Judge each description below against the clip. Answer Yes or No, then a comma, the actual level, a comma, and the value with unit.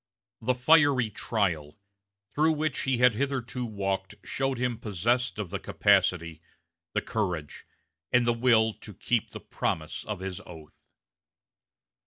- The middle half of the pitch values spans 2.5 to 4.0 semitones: No, average, 4.7 semitones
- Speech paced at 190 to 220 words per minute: No, slow, 135 wpm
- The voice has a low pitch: Yes, low, 110 Hz